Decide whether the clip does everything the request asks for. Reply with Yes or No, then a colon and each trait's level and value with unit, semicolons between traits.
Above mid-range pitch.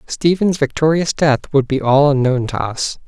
No: medium, 140 Hz